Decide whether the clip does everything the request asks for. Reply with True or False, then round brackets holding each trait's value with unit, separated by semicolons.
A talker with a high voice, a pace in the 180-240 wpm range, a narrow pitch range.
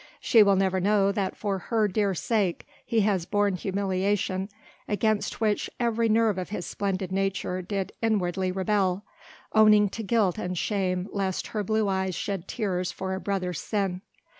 False (195 Hz; 165 wpm; 2.2 semitones)